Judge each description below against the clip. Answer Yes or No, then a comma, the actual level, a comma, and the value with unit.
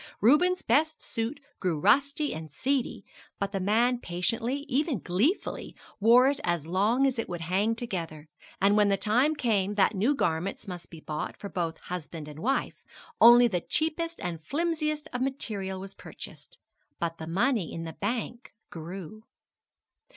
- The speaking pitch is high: Yes, high, 210 Hz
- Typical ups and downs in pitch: No, wide, 7.1 semitones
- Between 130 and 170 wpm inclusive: Yes, average, 160 wpm